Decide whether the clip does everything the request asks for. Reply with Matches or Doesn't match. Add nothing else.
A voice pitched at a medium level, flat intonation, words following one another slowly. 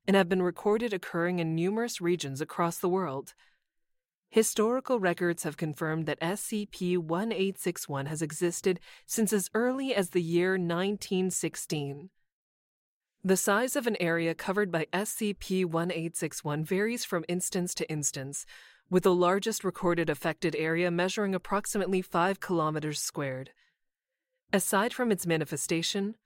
Doesn't match